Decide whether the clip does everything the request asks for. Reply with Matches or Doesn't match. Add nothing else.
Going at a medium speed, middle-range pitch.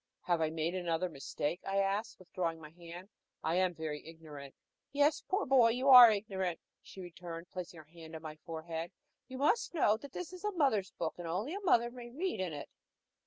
Doesn't match